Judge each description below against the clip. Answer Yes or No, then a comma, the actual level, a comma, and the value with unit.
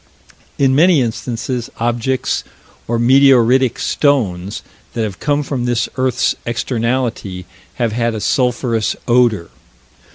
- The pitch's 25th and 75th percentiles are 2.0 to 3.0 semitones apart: Yes, narrow, 2.5 semitones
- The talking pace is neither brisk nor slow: No, slow, 110 wpm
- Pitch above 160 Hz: No, low, 120 Hz